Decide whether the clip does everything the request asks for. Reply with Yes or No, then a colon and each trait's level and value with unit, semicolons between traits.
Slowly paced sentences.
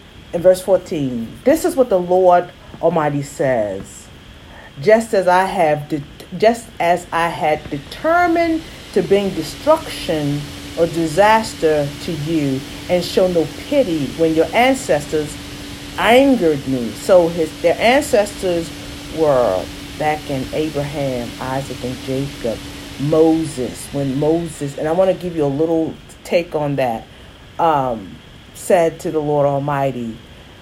Yes: slow, 125 wpm